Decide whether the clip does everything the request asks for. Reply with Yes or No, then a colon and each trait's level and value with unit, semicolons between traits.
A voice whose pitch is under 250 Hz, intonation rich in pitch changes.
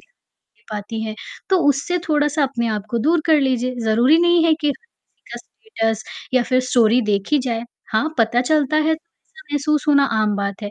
No: very high, 270 Hz; wide, 5.7 semitones